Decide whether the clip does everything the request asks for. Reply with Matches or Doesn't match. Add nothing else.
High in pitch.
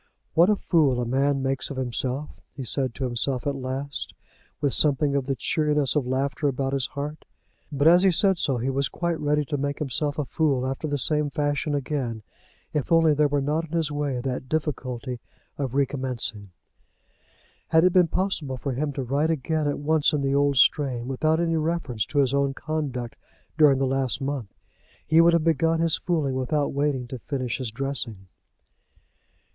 Doesn't match